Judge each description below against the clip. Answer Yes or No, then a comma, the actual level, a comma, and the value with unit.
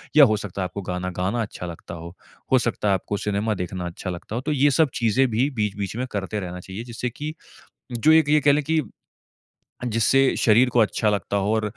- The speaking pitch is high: No, low, 110 Hz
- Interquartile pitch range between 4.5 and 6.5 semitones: Yes, average, 5.0 semitones